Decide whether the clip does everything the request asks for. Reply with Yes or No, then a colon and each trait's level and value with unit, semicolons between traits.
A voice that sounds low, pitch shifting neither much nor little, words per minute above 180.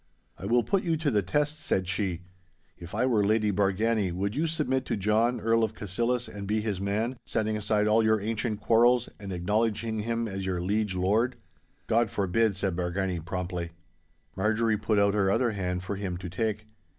Yes: low, 105 Hz; average, 3.0 semitones; average, 190 wpm